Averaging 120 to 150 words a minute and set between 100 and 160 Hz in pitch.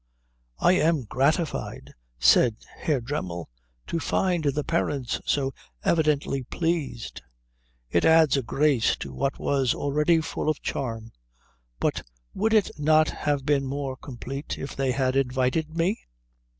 Yes: slow, 135 wpm; medium, 140 Hz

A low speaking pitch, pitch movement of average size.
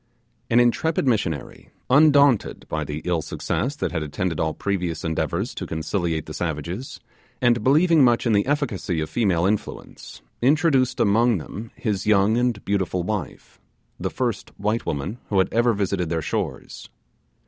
No: low, 105 Hz; wide, 5.9 semitones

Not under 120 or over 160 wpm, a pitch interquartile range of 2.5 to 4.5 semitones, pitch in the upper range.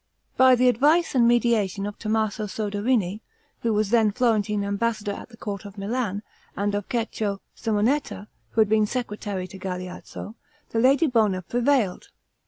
Yes: average, 155 wpm; average, 2.9 semitones; high, 215 Hz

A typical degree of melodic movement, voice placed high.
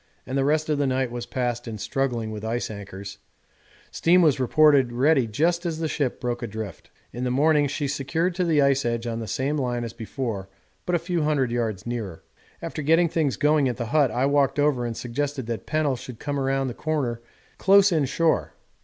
No: average, 4.3 semitones; low, 135 Hz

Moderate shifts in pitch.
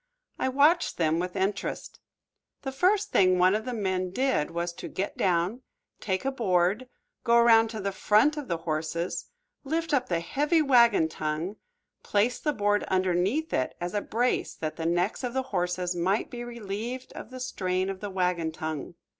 No: wide, 6.0 semitones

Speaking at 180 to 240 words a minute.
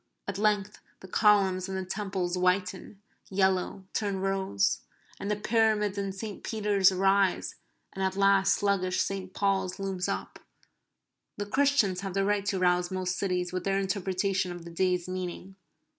No: average, 160 wpm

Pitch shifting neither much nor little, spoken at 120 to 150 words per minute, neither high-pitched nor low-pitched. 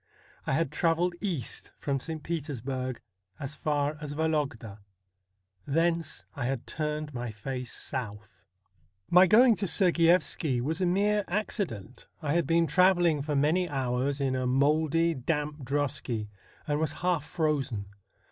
Yes: average, 4.1 semitones; average, 140 wpm; medium, 150 Hz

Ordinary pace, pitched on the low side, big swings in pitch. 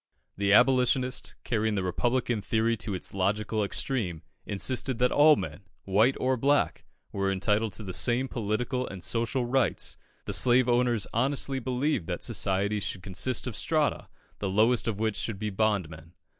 No: average, 160 wpm; low, 115 Hz; average, 4.1 semitones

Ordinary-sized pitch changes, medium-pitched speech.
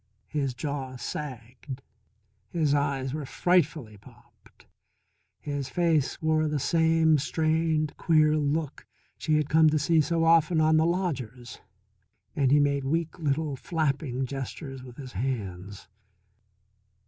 Yes: average, 3.1 semitones; medium, 150 Hz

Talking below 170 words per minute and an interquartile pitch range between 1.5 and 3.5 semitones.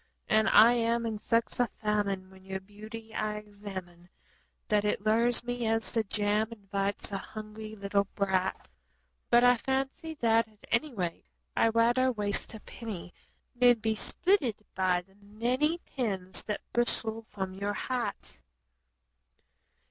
Yes: average, 145 wpm; average, 2.7 semitones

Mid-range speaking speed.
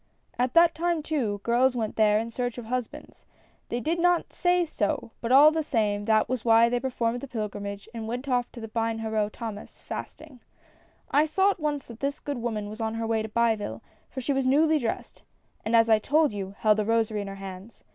No: fast, 215 wpm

